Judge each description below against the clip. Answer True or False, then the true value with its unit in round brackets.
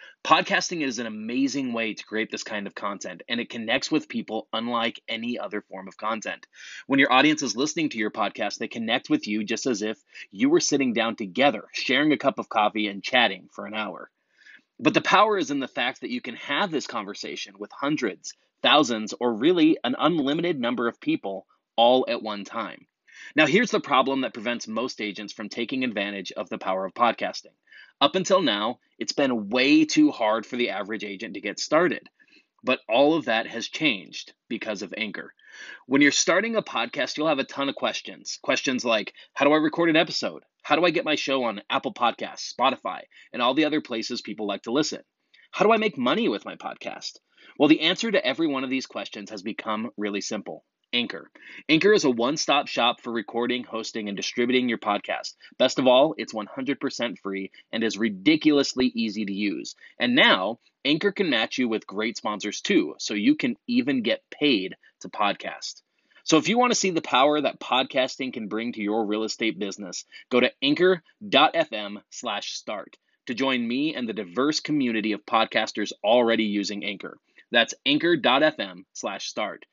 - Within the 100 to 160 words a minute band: False (195 wpm)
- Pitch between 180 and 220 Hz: False (125 Hz)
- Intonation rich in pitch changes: True (8.7 semitones)